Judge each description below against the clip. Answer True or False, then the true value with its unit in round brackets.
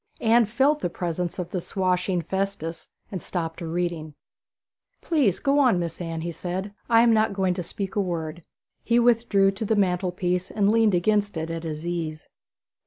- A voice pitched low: False (185 Hz)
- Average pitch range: True (3.8 semitones)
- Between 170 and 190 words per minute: True (180 wpm)